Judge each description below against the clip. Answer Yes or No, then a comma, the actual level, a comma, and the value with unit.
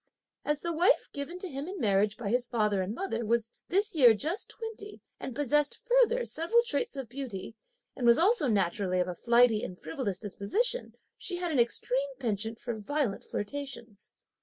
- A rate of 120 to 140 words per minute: No, average, 180 wpm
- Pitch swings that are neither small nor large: No, wide, 8.0 semitones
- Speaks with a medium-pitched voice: No, very high, 255 Hz